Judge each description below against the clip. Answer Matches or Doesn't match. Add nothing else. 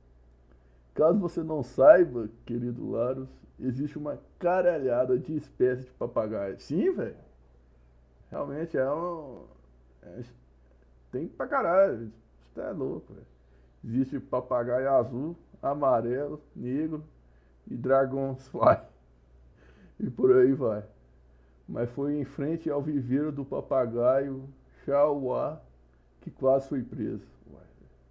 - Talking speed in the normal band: Doesn't match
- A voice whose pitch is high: Doesn't match